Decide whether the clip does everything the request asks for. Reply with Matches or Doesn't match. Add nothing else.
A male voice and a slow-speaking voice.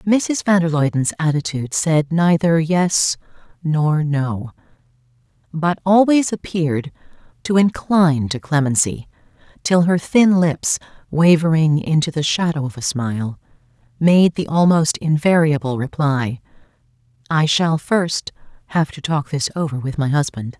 Doesn't match